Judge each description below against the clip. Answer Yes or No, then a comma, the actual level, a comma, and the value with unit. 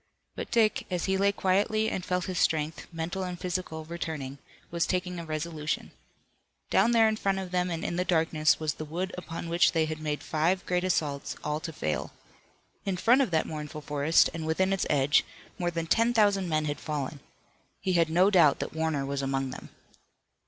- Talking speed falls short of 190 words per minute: No, average, 200 wpm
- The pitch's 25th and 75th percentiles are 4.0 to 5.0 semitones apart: No, average, 3.2 semitones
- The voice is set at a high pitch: No, medium, 165 Hz